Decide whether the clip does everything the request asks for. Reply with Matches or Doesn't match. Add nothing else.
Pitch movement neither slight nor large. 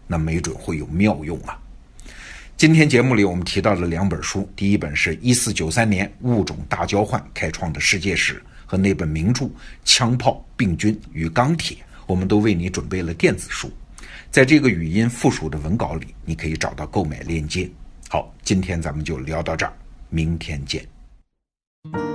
Matches